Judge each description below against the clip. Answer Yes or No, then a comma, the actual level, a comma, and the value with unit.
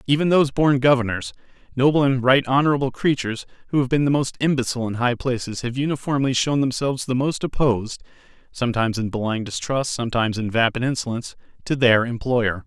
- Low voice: Yes, low, 125 Hz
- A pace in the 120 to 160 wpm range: No, average, 170 wpm